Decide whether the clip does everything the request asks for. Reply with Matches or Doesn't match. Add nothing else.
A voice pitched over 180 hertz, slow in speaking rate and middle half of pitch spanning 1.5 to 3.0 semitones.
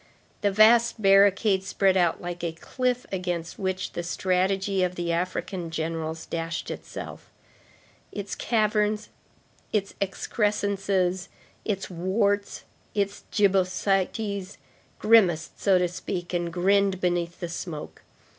Matches